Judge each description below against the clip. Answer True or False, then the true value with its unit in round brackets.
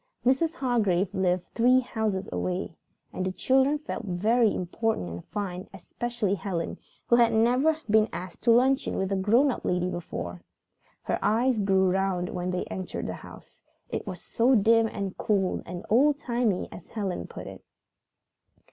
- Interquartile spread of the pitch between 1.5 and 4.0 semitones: False (4.6 semitones)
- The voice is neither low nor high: False (205 Hz)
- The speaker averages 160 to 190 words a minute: True (165 wpm)